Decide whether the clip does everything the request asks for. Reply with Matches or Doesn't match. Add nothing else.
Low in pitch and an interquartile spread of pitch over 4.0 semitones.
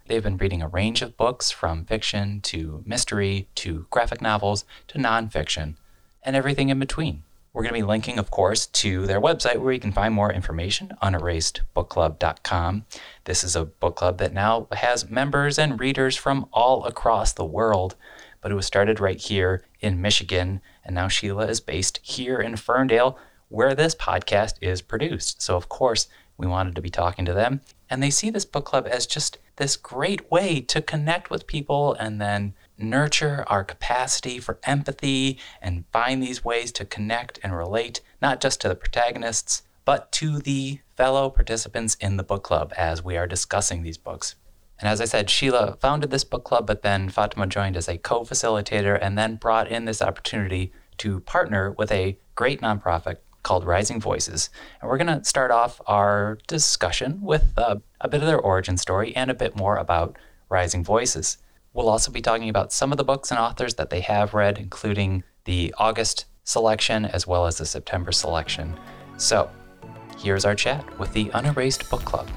Matches